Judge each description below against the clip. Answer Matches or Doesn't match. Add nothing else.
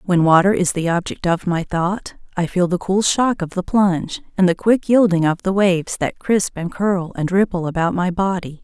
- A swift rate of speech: Matches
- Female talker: Matches